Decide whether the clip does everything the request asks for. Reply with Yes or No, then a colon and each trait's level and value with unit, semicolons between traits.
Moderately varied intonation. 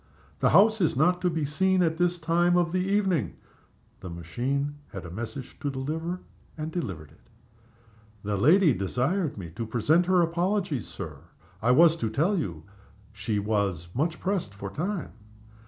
No: wide, 8.6 semitones